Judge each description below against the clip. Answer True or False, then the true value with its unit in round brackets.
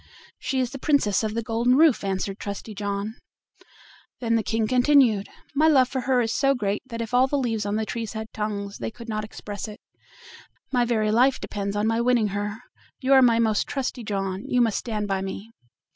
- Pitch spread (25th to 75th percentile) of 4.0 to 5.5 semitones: False (3.3 semitones)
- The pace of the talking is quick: True (210 wpm)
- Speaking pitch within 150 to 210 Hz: False (225 Hz)